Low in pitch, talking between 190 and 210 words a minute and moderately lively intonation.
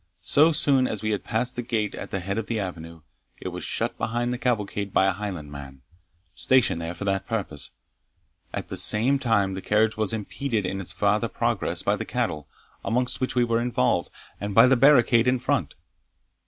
Yes: low, 110 Hz; average, 200 wpm; average, 4.1 semitones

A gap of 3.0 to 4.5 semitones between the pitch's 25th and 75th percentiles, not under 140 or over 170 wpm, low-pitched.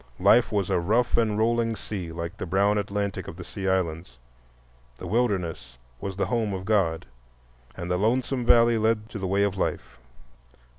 No: average, 3.6 semitones; average, 180 wpm; low, 100 Hz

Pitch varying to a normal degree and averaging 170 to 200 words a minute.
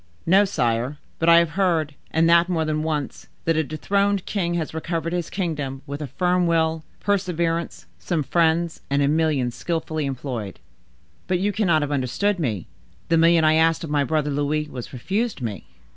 Yes: average, 3.0 semitones; average, 175 wpm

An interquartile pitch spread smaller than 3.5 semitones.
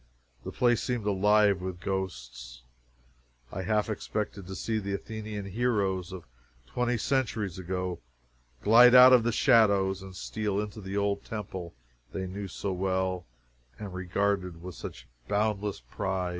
Yes: narrow, 2.5 semitones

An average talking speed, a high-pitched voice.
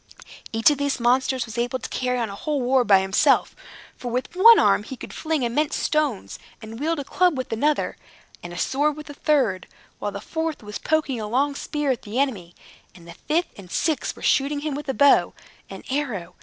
No: fast, 215 wpm; very high, 265 Hz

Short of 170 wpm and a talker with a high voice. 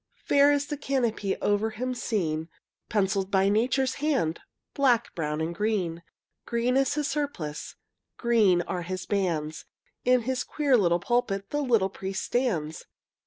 Yes: average, 145 wpm; high, 215 Hz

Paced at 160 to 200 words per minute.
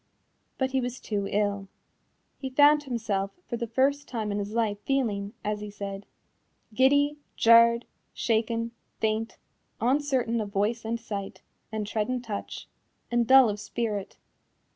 No: average, 145 wpm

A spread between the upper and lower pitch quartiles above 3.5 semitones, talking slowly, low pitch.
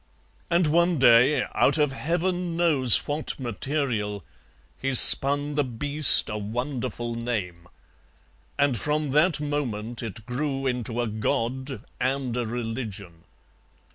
Yes: average, 4.3 semitones; slow, 120 wpm; low, 130 Hz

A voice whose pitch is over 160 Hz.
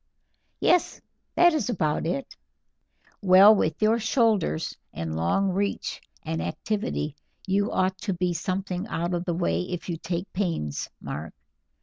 Yes: medium, 185 Hz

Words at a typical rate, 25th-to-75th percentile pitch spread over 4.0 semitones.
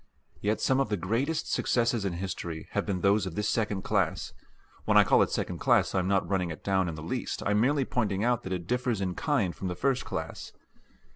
No: fast, 235 wpm; average, 4.7 semitones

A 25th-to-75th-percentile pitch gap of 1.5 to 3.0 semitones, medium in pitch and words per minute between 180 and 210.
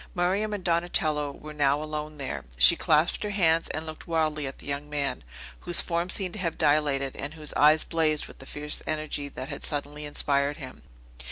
Yes: narrow, 2.4 semitones; medium, 150 Hz; average, 195 wpm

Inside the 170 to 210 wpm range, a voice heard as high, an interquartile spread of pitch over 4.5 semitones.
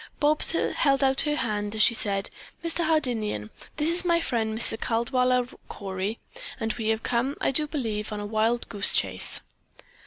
Yes: average, 175 wpm; high, 235 Hz; average, 4.9 semitones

